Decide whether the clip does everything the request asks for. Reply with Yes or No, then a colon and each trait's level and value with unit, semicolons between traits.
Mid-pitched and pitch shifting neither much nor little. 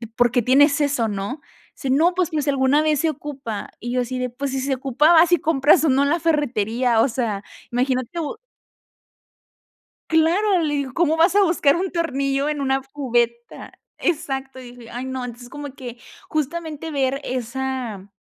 No: very high, 275 Hz; average, 3.7 semitones